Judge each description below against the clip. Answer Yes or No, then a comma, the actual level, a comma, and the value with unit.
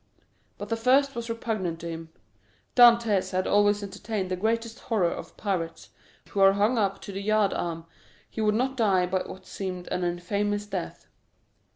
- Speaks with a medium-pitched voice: No, high, 205 Hz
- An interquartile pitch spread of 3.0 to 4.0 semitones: Yes, average, 3.3 semitones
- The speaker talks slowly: No, average, 175 wpm